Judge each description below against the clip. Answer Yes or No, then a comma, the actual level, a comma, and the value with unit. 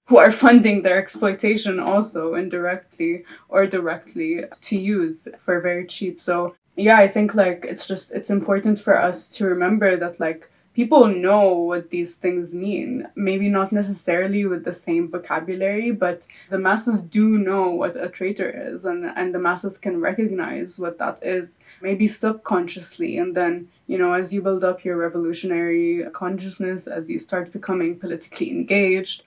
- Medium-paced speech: Yes, average, 160 wpm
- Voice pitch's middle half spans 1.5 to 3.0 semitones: Yes, narrow, 2.5 semitones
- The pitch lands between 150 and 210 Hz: Yes, medium, 185 Hz